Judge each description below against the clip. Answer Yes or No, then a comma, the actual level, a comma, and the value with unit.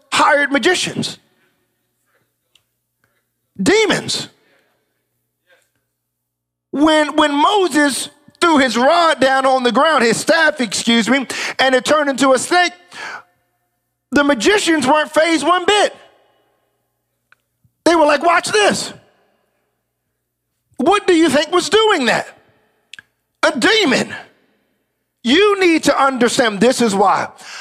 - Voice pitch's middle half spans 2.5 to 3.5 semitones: No, average, 4.5 semitones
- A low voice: No, very high, 295 Hz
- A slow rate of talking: Yes, slow, 110 wpm